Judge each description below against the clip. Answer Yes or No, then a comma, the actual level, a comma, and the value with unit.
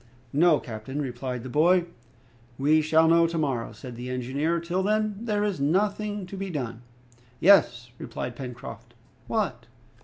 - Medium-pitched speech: Yes, medium, 155 Hz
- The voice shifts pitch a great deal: Yes, wide, 6.6 semitones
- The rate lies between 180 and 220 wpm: No, average, 150 wpm